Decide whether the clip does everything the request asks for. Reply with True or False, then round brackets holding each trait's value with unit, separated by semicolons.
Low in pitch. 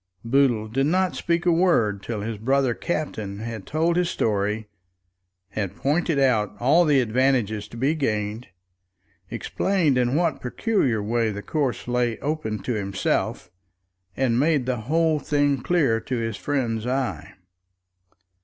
True (125 Hz)